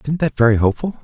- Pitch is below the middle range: Yes, low, 130 Hz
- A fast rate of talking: Yes, fast, 230 wpm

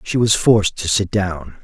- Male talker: Yes, male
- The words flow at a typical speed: No, fast, 220 wpm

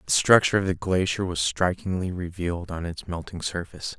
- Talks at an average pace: Yes, average, 180 wpm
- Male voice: Yes, male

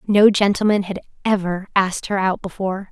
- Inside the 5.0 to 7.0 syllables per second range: Yes, 5.6 syllables/s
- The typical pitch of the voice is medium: No, high, 195 Hz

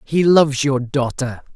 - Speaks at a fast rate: No, average, 155 wpm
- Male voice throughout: Yes, male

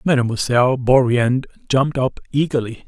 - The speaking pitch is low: Yes, low, 130 Hz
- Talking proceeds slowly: Yes, slow, 105 wpm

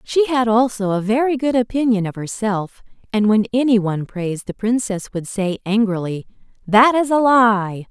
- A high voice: Yes, high, 220 Hz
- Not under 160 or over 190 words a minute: Yes, average, 175 wpm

